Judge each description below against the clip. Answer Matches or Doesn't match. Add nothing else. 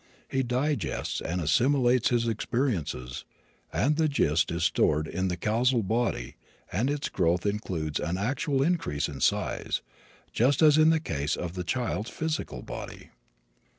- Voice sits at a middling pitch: Doesn't match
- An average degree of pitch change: Doesn't match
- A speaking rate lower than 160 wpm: Matches